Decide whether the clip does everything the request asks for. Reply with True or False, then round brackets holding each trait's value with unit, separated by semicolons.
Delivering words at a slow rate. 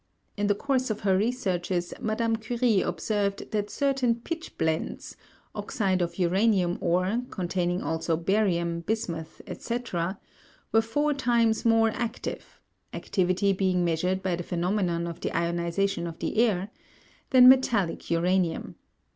True (130 wpm)